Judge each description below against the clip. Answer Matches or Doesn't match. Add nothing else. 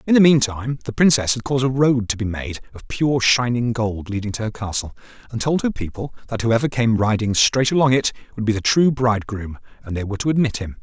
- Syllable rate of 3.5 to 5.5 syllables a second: Doesn't match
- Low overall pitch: Matches